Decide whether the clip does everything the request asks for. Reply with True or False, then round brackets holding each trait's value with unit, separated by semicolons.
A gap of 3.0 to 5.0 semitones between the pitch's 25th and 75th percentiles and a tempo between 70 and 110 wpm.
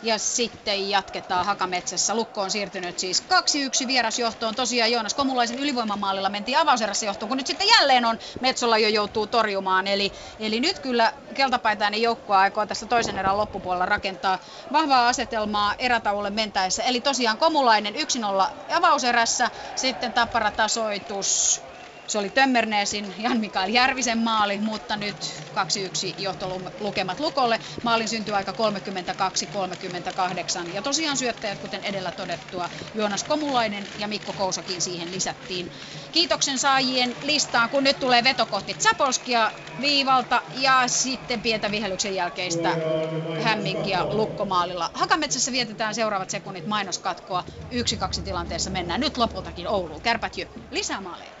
False (4.2 semitones; 130 wpm)